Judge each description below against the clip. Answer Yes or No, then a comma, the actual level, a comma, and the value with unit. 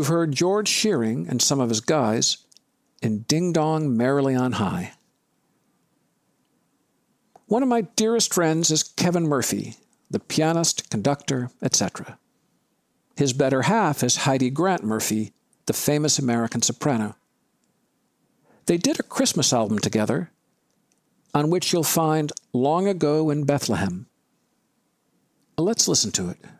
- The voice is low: No, medium, 145 Hz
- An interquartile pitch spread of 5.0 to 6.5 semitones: Yes, wide, 5.4 semitones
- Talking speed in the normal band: No, slow, 125 wpm